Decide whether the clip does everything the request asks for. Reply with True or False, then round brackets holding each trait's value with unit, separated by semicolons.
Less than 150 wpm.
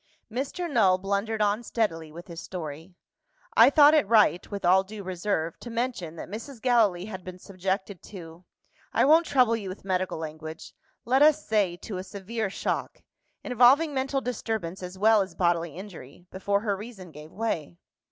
False (170 wpm)